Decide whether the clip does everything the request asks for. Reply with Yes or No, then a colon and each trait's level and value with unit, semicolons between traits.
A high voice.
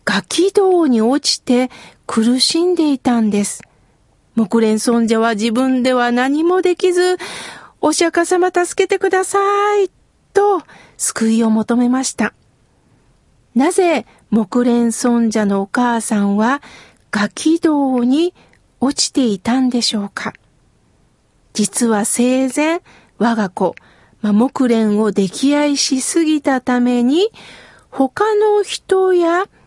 Yes: very high, 260 Hz